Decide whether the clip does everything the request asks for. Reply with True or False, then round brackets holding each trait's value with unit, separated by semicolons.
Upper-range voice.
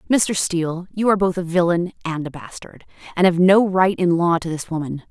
False (175 Hz)